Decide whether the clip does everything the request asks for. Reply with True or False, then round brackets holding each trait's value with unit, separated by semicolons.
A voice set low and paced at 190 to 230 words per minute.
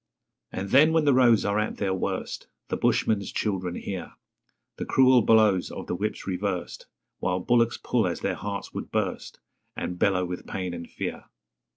False (100 Hz; 175 wpm)